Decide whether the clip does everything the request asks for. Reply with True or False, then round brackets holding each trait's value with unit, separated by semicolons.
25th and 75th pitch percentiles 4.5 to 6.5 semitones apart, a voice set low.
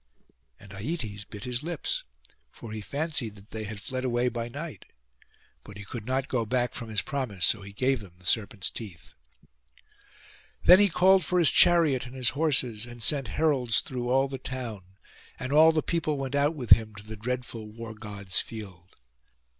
True (4.8 semitones; 120 Hz)